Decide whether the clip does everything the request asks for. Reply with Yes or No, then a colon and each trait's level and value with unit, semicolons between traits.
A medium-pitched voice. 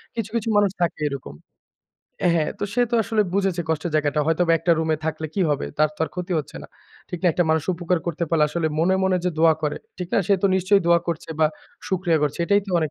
Yes: medium, 170 Hz